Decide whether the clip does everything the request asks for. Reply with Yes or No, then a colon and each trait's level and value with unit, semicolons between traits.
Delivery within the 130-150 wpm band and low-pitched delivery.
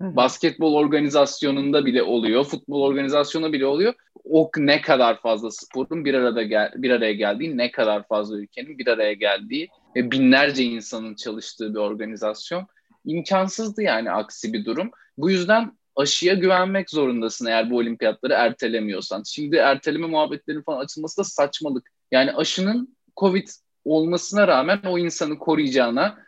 No: fast, 140 wpm; medium, 145 Hz